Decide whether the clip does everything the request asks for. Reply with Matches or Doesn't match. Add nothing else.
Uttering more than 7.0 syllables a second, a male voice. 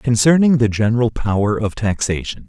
Doesn't match